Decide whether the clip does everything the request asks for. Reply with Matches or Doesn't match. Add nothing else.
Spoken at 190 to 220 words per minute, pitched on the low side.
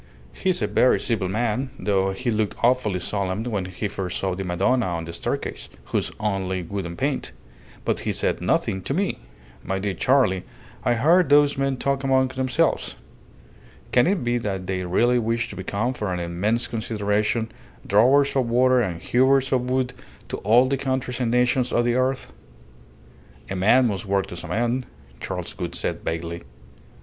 Doesn't match